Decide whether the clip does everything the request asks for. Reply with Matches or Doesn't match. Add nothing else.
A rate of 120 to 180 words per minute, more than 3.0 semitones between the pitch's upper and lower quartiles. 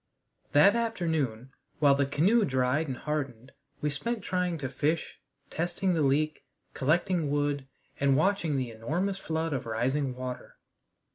Matches